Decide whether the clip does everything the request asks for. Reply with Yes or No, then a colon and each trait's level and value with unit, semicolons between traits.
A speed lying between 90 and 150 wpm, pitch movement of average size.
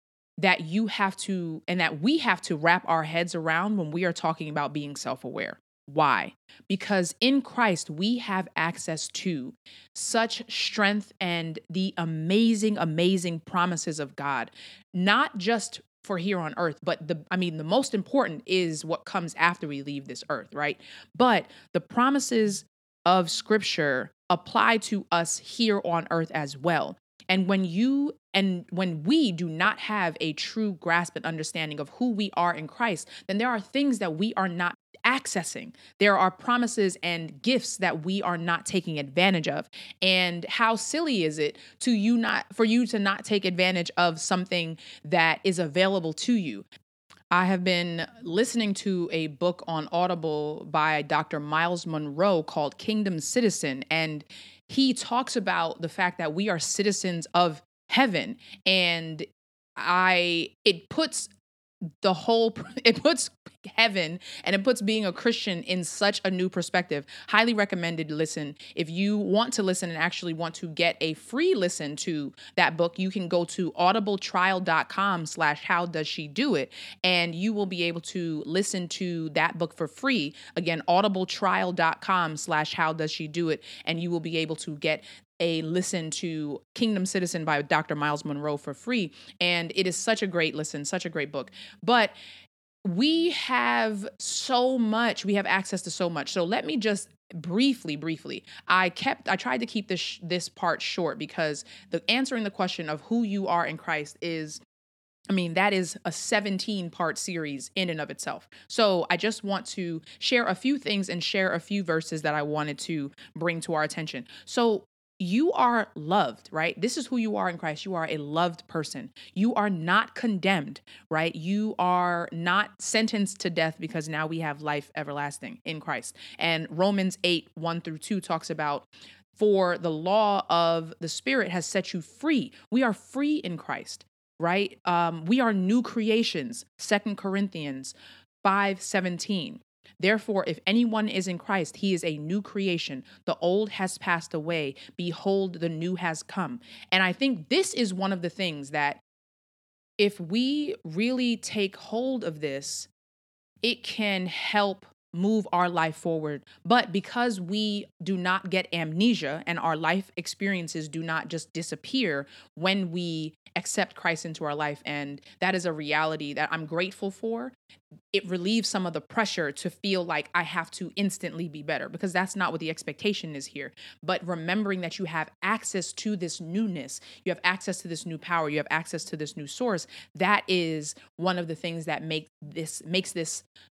No: average, 175 wpm; average, 4.0 semitones